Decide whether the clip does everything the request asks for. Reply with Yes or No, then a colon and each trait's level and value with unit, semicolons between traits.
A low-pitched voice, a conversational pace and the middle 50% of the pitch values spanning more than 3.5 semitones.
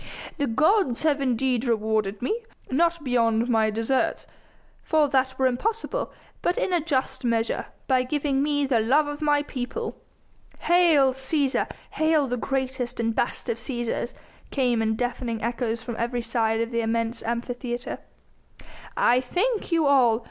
No: very high, 255 Hz; average, 150 wpm; average, 3.9 semitones